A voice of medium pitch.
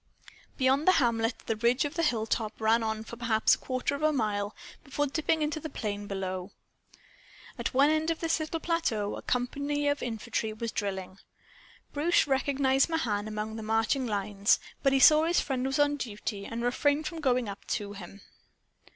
No: high, 245 Hz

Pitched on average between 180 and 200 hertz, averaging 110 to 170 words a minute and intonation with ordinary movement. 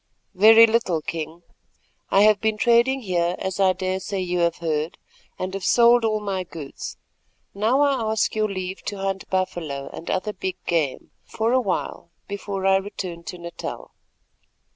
Yes: high, 190 Hz; average, 165 wpm; average, 3.6 semitones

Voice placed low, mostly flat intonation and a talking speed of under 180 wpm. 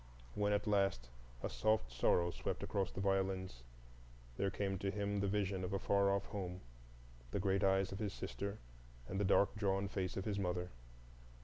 No: very low, 95 Hz; narrow, 1.3 semitones; average, 185 wpm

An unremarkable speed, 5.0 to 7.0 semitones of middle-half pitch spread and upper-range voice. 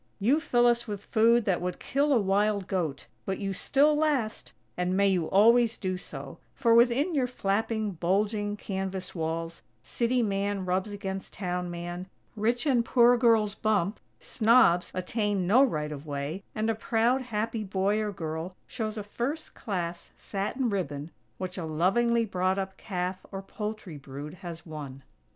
No: average, 165 wpm; average, 4.3 semitones; high, 200 Hz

